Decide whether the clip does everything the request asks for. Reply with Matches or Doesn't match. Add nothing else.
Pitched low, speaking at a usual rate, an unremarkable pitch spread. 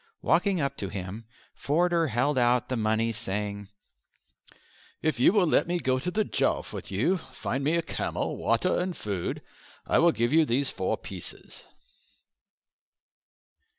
Doesn't match